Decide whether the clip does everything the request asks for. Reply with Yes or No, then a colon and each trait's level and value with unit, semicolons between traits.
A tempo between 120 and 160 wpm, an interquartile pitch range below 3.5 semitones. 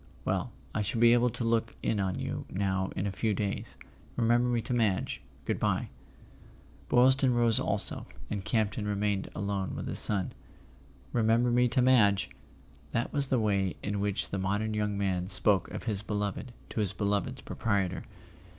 No: average, 170 wpm; average, 3.0 semitones